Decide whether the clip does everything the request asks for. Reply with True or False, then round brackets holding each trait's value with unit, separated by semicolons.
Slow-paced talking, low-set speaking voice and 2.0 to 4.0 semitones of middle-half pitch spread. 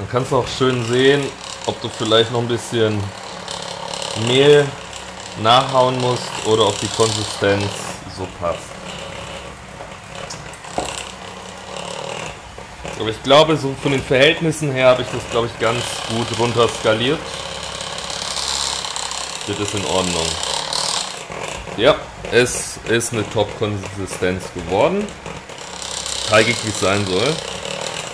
True (115 wpm; 115 Hz; 3.7 semitones)